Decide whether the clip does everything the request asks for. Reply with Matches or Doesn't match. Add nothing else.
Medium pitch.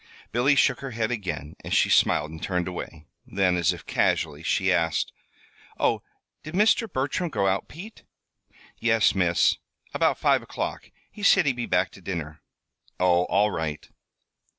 Doesn't match